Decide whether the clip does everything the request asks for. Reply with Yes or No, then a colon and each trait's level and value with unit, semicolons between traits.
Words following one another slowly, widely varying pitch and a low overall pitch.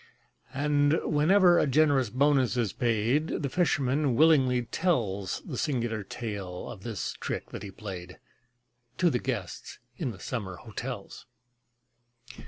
Yes: slow, 130 wpm; wide, 5.8 semitones; low, 125 Hz